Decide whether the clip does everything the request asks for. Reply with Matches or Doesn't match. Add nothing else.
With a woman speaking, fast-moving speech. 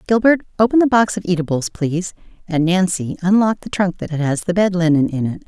Matches